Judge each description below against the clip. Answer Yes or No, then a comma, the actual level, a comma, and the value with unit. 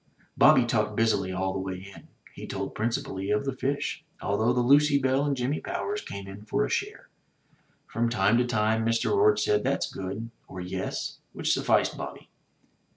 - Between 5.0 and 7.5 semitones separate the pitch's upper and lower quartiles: Yes, wide, 5.4 semitones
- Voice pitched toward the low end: Yes, low, 115 Hz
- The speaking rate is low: No, average, 180 wpm